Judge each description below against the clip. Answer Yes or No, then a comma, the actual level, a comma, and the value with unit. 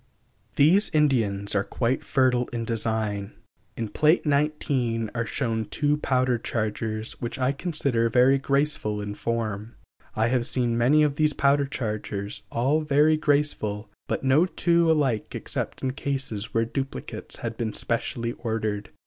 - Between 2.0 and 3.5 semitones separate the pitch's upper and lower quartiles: No, average, 4.2 semitones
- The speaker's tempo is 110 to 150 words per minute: Yes, average, 145 wpm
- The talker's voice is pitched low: Yes, low, 120 Hz